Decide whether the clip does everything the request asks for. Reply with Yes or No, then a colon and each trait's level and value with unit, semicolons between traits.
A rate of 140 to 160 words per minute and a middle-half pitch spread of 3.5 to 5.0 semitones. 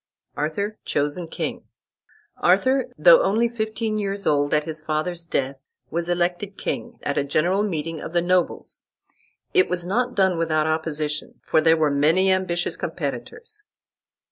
Yes: average, 145 wpm; average, 4.6 semitones